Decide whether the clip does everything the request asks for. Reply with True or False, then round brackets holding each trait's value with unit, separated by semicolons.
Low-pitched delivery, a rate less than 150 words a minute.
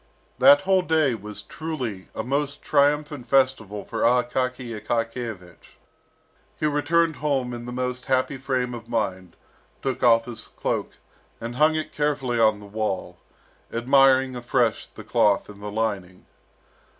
True (125 Hz; 140 wpm)